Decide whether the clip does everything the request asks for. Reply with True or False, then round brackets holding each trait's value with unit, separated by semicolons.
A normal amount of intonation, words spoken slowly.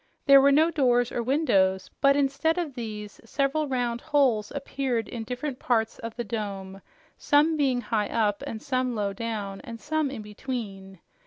False (4.6 semitones; 170 wpm)